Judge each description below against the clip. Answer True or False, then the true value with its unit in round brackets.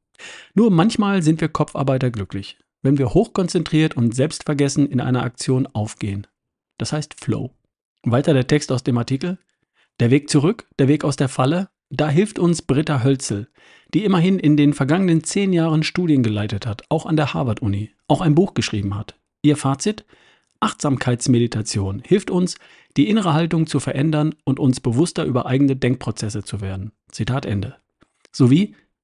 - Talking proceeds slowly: False (160 wpm)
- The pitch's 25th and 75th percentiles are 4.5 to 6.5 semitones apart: True (5.1 semitones)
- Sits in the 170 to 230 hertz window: False (140 Hz)